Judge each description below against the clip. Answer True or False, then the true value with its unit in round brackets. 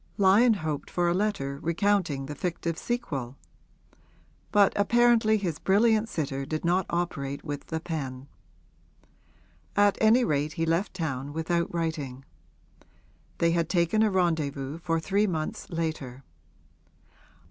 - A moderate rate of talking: False (125 wpm)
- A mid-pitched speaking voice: True (165 Hz)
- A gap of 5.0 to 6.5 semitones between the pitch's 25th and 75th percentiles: True (5.3 semitones)